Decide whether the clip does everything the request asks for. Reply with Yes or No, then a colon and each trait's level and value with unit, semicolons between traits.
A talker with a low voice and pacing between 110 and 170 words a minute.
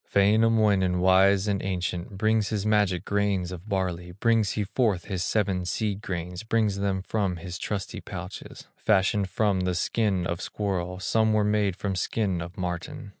Yes: low, 100 Hz; average, 165 wpm